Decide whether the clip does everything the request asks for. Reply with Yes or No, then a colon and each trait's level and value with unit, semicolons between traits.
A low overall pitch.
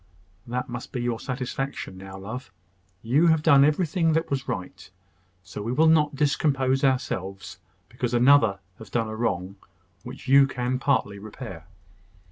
Yes: low, 125 Hz